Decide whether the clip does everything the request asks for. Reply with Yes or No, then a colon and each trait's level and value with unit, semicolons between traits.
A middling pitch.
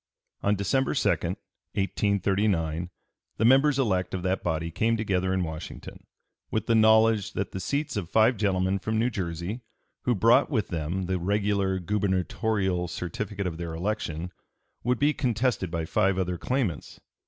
No: low, 100 Hz